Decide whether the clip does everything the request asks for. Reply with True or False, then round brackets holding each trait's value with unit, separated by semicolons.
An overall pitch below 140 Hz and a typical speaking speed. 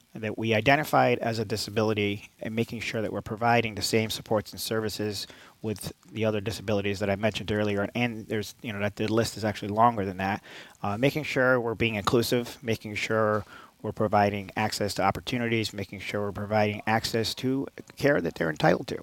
True (110 Hz; 190 wpm)